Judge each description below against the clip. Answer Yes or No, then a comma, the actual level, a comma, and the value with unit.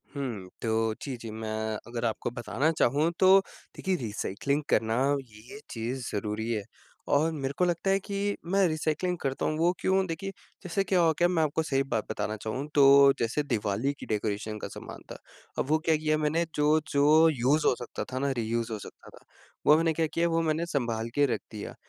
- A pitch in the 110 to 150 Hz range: Yes, medium, 140 Hz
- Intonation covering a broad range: Yes, wide, 6.1 semitones